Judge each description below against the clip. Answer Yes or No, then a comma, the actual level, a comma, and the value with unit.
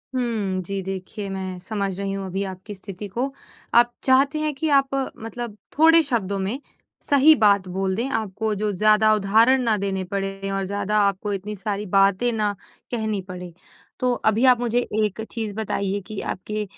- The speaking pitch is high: Yes, high, 210 Hz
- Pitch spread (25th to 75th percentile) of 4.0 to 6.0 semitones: No, average, 3.0 semitones